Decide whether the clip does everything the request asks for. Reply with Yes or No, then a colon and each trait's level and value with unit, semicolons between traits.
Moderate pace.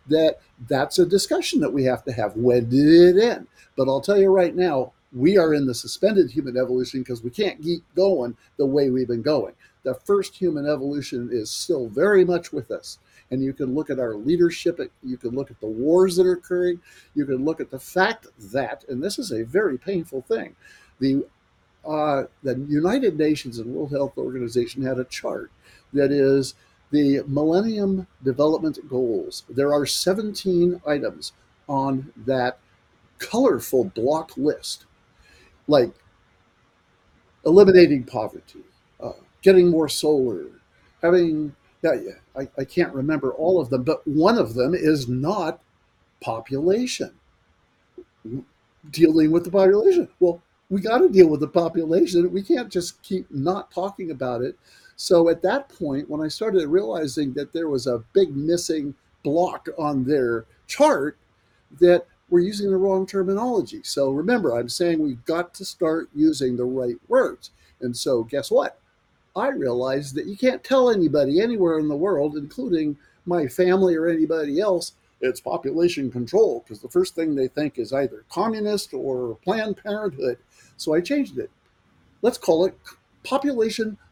Yes: average, 160 wpm